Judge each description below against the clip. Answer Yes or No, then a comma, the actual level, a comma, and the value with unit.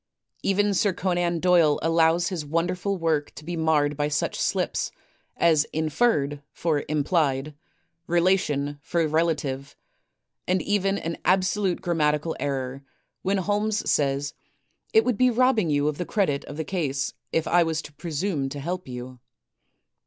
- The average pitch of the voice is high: No, medium, 165 Hz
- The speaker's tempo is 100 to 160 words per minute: Yes, average, 145 wpm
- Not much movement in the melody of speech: No, average, 4.0 semitones